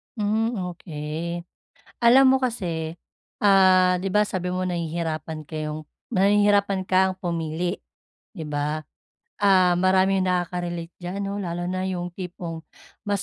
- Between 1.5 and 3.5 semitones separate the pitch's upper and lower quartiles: Yes, narrow, 2.6 semitones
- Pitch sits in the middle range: Yes, medium, 180 Hz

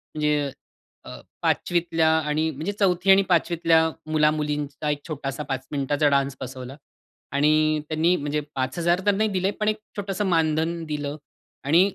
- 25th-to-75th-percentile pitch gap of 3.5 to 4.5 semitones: No, average, 3.0 semitones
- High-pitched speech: No, medium, 155 Hz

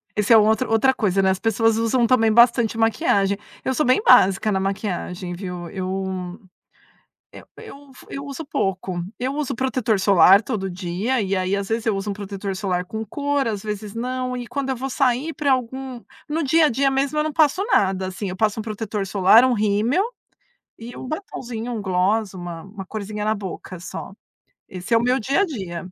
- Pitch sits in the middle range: No, high, 220 Hz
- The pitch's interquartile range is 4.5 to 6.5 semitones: Yes, average, 4.9 semitones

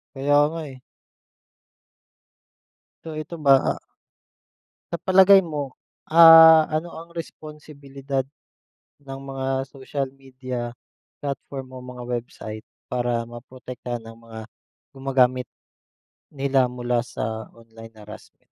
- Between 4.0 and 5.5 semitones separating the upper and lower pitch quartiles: No, average, 3.0 semitones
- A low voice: Yes, low, 130 Hz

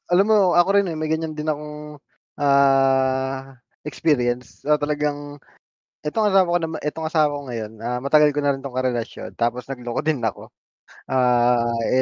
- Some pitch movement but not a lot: Yes, average, 3.3 semitones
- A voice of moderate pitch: Yes, medium, 145 Hz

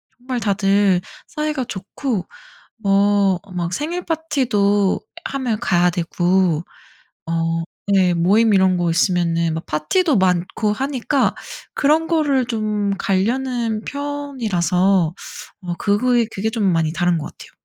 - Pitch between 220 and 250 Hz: No, high, 200 Hz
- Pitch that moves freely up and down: Yes, wide, 6.1 semitones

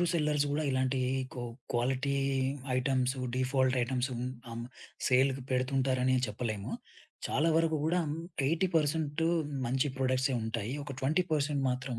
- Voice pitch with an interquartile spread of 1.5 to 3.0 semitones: Yes, narrow, 2.5 semitones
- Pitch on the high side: No, low, 135 Hz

